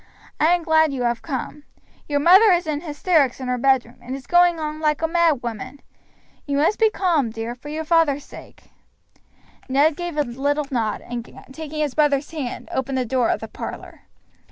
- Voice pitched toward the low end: No, very high, 290 Hz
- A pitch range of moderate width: Yes, average, 3.7 semitones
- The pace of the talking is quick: No, average, 195 wpm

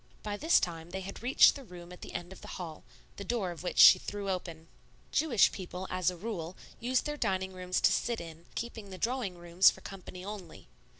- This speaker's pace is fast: Yes, fast, 220 wpm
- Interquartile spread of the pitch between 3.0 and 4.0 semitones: Yes, average, 3.3 semitones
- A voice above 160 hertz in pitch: Yes, medium, 185 Hz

